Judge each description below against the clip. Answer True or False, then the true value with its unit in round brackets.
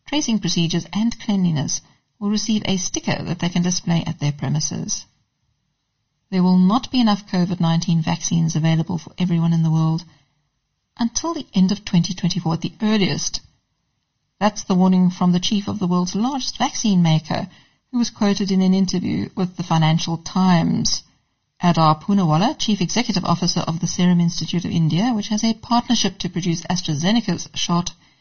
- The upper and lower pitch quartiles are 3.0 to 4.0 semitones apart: True (3.7 semitones)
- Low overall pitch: False (180 Hz)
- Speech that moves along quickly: False (165 wpm)